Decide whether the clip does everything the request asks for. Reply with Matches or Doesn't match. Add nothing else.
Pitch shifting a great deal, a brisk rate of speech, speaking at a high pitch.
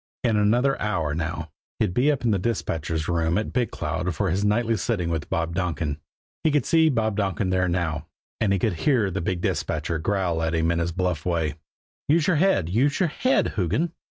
Doesn't match